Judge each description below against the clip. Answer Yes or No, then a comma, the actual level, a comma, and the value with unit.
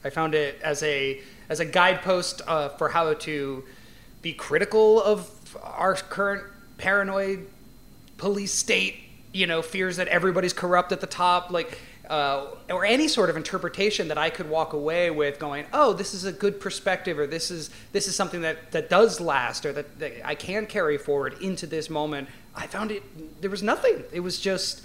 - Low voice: No, medium, 180 Hz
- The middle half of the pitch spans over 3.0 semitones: Yes, average, 4.3 semitones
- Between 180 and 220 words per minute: Yes, average, 190 wpm